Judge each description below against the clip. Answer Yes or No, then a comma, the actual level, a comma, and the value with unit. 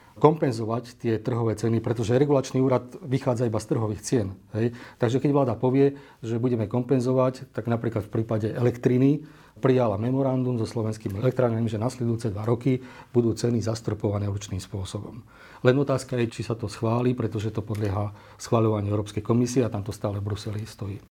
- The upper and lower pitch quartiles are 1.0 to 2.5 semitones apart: No, average, 2.9 semitones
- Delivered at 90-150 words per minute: No, fast, 165 wpm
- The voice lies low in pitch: Yes, low, 115 Hz